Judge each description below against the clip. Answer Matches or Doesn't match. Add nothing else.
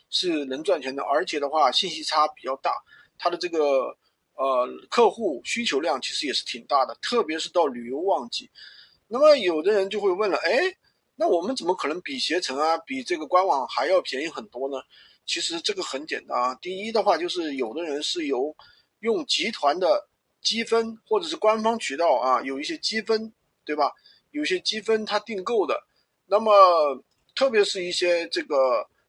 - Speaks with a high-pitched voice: Matches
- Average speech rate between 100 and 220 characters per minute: Doesn't match